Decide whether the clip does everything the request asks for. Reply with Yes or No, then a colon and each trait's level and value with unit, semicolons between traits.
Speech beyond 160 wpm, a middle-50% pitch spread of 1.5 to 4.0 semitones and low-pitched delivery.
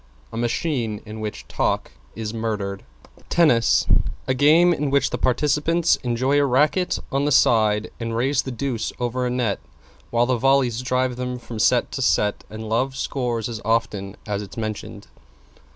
Yes: average, 170 wpm; average, 3.6 semitones; low, 120 Hz